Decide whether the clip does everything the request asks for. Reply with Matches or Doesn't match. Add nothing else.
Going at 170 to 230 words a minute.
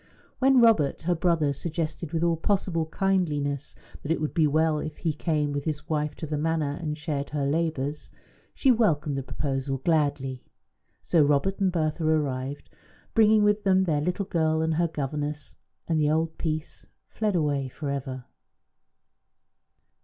Doesn't match